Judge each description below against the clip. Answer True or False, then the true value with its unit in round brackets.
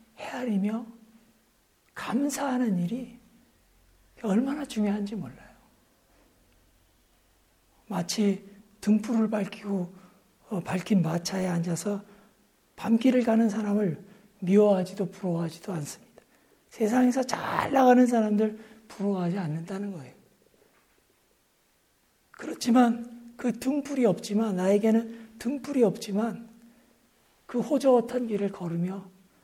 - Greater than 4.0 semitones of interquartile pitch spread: False (3.6 semitones)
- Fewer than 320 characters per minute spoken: True (230 characters per minute)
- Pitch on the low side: False (210 Hz)